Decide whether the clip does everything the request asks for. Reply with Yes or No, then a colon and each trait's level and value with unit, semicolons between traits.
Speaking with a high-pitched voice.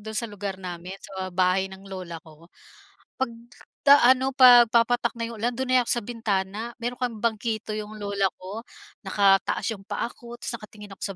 Yes: high, 215 Hz